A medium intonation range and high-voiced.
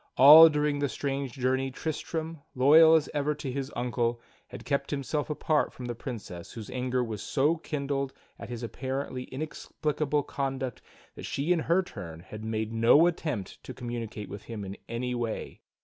No: average, 3.9 semitones; low, 135 Hz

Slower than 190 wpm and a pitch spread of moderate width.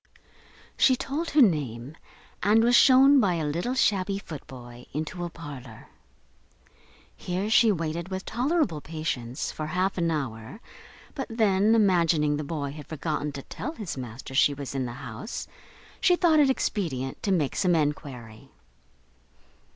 No: average, 150 wpm; wide, 7.1 semitones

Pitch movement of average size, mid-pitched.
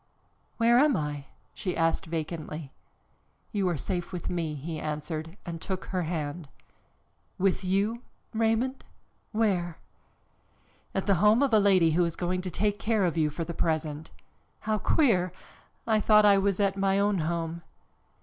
Yes: average, 4.0 semitones; medium, 180 Hz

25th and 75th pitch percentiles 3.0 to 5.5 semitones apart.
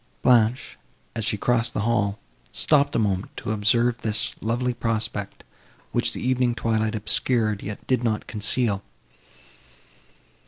No: narrow, 2.4 semitones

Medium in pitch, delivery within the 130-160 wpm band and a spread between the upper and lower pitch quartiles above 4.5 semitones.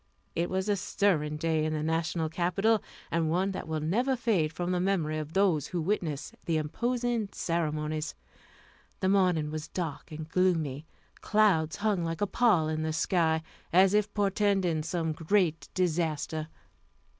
No: medium, 170 Hz; average, 155 wpm; average, 3.8 semitones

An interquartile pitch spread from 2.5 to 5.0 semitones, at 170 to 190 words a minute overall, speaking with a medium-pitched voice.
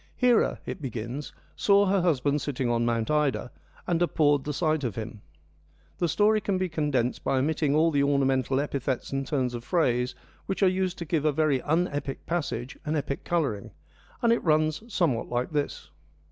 Yes: average, 4.5 semitones; average, 185 wpm; medium, 145 Hz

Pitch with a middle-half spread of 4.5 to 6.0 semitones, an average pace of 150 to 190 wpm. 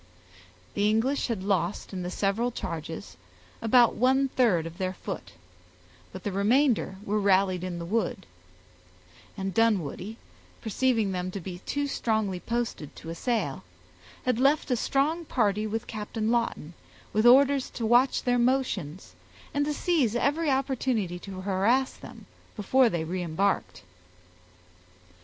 No: average, 5.2 semitones; average, 140 wpm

